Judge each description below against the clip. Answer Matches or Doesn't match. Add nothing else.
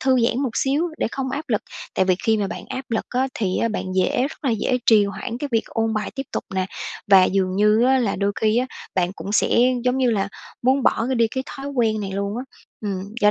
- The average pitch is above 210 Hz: Matches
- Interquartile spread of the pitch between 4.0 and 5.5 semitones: Matches